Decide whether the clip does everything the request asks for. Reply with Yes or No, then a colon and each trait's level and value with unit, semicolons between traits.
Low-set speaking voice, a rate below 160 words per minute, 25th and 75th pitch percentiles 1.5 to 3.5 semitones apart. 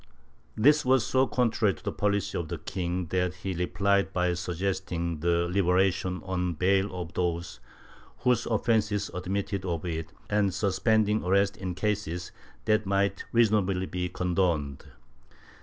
Yes: very low, 95 Hz; average, 140 wpm; narrow, 2.5 semitones